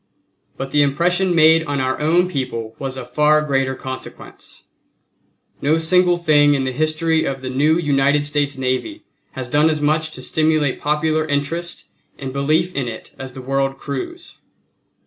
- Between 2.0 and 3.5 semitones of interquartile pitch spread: Yes, average, 3.0 semitones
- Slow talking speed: No, average, 165 wpm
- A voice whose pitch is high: No, medium, 145 Hz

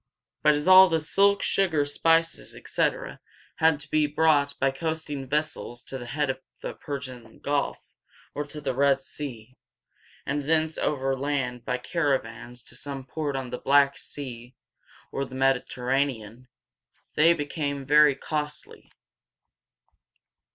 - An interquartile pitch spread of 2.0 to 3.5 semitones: Yes, narrow, 2.6 semitones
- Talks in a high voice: No, medium, 140 Hz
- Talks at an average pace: No, slow, 130 wpm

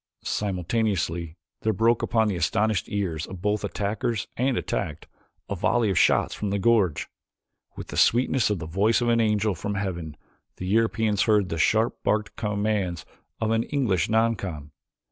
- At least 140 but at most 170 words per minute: Yes, average, 165 wpm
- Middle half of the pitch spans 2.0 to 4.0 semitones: Yes, average, 3.3 semitones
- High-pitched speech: No, low, 105 Hz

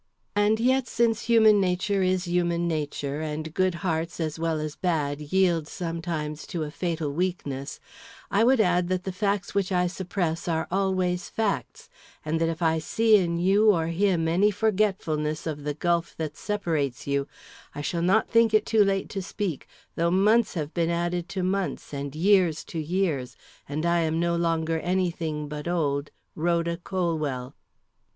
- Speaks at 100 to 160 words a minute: No, average, 175 wpm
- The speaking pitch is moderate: Yes, medium, 170 Hz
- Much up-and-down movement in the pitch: No, average, 3.4 semitones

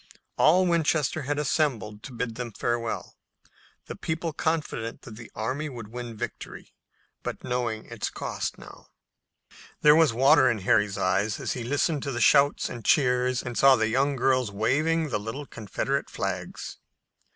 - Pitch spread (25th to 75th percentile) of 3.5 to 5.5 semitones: Yes, average, 4.5 semitones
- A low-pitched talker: Yes, low, 125 Hz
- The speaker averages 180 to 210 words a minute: No, average, 160 wpm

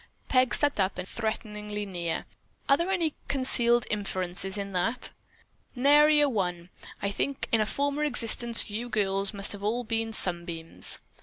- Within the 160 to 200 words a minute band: No, average, 150 wpm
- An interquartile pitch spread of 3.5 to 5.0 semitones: Yes, average, 4.7 semitones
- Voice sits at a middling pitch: No, high, 215 Hz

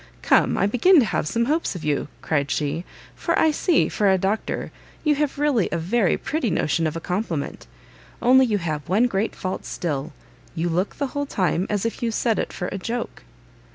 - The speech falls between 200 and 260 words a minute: Yes, fast, 205 wpm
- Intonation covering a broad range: Yes, wide, 6.7 semitones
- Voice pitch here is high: Yes, high, 200 Hz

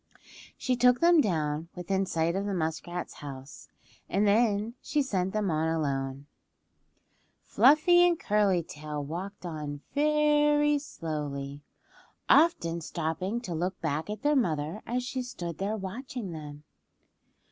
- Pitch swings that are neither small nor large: No, wide, 7.8 semitones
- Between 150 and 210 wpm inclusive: No, slow, 135 wpm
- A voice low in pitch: No, medium, 185 Hz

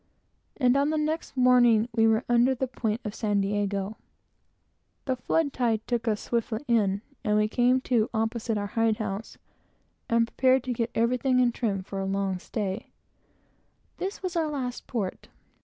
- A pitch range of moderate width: Yes, average, 3.1 semitones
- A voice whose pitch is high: Yes, high, 230 Hz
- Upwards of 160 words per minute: Yes, average, 175 wpm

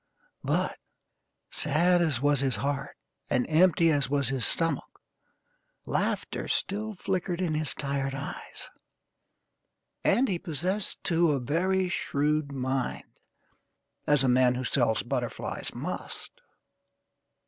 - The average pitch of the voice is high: No, medium, 145 Hz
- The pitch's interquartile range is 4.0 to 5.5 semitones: Yes, average, 4.4 semitones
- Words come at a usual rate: No, slow, 115 wpm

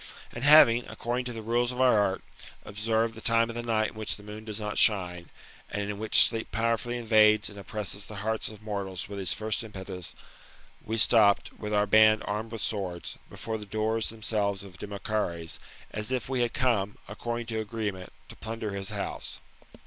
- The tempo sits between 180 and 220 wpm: Yes, average, 190 wpm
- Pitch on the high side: No, low, 110 Hz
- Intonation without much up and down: Yes, narrow, 1.9 semitones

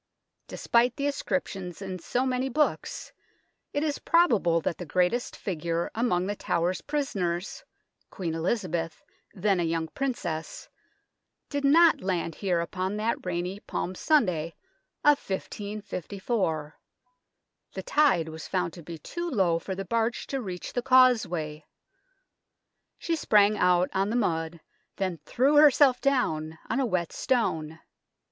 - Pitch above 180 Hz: Yes, high, 190 Hz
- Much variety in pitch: Yes, wide, 6.7 semitones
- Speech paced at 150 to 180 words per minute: No, slow, 135 wpm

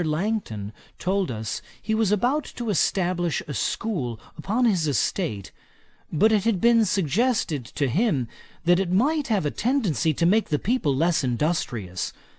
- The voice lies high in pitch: No, medium, 180 Hz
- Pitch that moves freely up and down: Yes, wide, 7.4 semitones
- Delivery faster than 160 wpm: No, average, 155 wpm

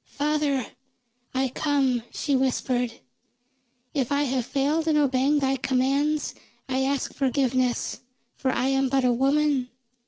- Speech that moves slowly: Yes, slow, 130 wpm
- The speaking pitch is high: Yes, very high, 270 Hz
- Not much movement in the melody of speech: Yes, narrow, 1.9 semitones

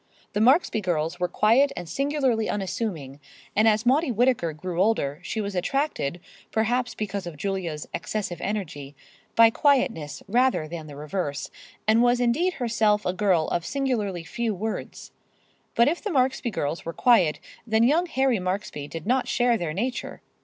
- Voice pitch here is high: Yes, high, 215 Hz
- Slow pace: No, average, 160 wpm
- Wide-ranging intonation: Yes, wide, 6.1 semitones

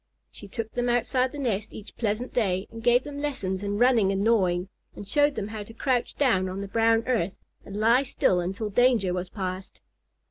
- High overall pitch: Yes, high, 220 Hz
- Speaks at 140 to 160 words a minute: No, fast, 205 wpm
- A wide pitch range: No, average, 4.1 semitones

